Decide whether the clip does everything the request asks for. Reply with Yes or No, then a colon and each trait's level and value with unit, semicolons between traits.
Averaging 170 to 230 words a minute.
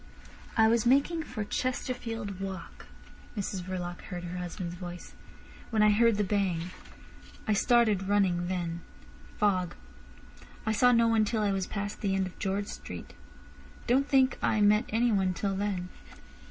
No: average, 155 wpm